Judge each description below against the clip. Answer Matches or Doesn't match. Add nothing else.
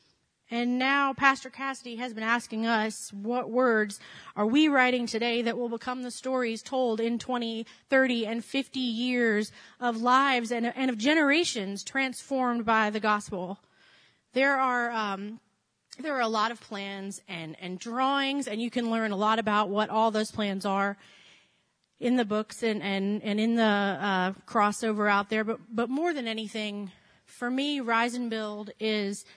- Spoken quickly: Doesn't match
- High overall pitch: Matches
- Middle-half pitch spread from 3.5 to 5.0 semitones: Doesn't match